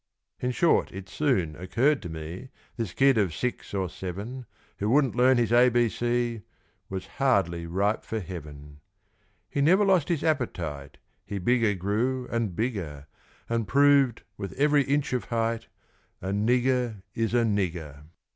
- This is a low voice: Yes, low, 115 Hz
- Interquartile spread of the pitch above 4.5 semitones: Yes, average, 5.3 semitones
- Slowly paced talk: No, average, 155 wpm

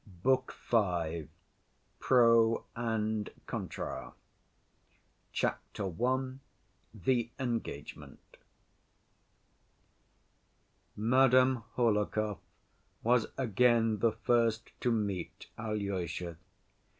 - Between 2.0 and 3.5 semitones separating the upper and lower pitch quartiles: Yes, average, 2.8 semitones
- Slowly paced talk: Yes, slow, 65 wpm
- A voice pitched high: No, low, 115 Hz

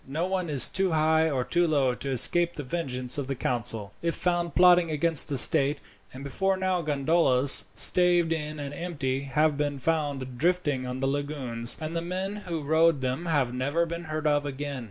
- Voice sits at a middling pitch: Yes, medium, 150 Hz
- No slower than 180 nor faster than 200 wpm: Yes, average, 195 wpm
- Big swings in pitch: No, average, 3.9 semitones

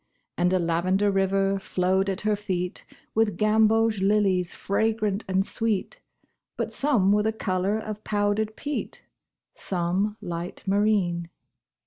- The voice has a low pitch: No, high, 200 Hz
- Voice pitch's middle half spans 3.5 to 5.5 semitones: No, narrow, 2.4 semitones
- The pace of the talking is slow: Yes, slow, 125 wpm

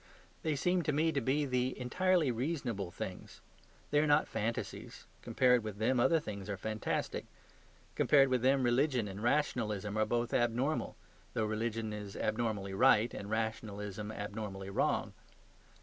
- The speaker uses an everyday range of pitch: Yes, average, 4.4 semitones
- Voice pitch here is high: No, low, 115 Hz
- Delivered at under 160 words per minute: Yes, average, 150 wpm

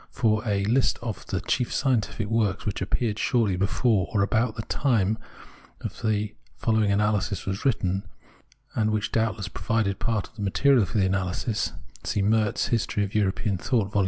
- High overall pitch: No, low, 105 Hz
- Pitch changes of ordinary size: No, narrow, 2.3 semitones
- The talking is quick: No, average, 165 wpm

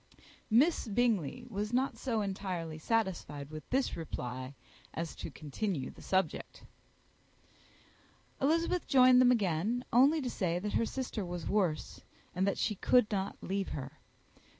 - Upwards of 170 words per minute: No, average, 140 wpm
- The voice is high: Yes, high, 200 Hz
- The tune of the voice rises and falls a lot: Yes, wide, 6.6 semitones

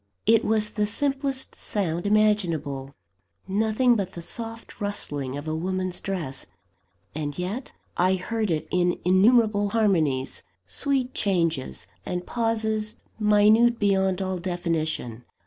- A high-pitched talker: Yes, high, 195 Hz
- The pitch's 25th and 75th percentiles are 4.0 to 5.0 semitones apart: Yes, average, 4.5 semitones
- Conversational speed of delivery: No, slow, 120 wpm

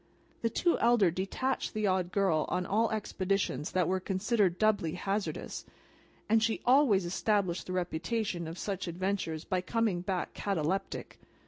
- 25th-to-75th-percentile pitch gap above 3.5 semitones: No, average, 3.2 semitones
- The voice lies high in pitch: Yes, high, 195 Hz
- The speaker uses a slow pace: No, average, 145 wpm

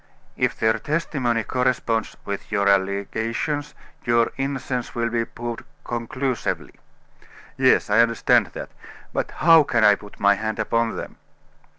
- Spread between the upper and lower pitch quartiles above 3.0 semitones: No, average, 2.7 semitones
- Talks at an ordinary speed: No, slow, 130 wpm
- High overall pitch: No, low, 115 Hz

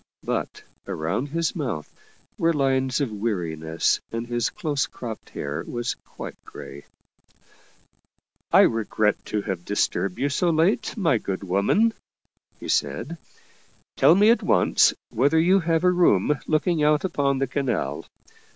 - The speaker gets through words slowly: No, average, 150 wpm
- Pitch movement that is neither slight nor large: No, wide, 7.7 semitones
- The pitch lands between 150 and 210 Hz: No, low, 135 Hz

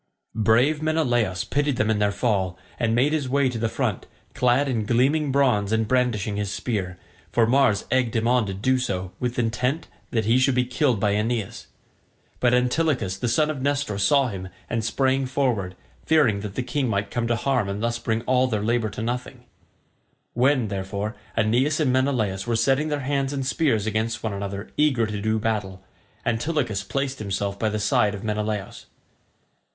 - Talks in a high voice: No, low, 115 Hz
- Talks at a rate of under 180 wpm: No, average, 185 wpm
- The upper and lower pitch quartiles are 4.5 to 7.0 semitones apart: No, average, 3.8 semitones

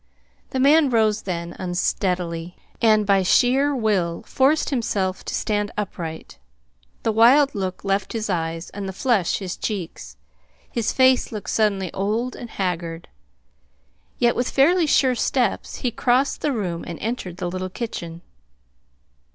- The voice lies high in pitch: Yes, high, 205 Hz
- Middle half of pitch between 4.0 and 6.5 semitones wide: Yes, average, 5.2 semitones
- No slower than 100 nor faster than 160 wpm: Yes, average, 145 wpm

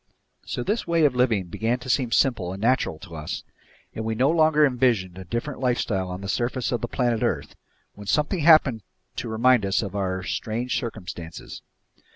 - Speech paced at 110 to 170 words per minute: No, average, 190 wpm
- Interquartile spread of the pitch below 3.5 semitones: No, average, 4.8 semitones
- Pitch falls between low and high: No, low, 120 Hz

